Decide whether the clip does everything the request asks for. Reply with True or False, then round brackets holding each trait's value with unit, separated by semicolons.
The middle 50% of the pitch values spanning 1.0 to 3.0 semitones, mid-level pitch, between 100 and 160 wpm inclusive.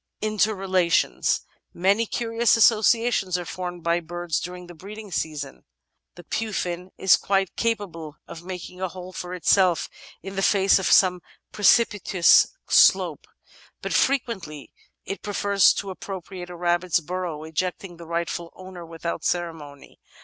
True (2.6 semitones; 180 Hz; 135 wpm)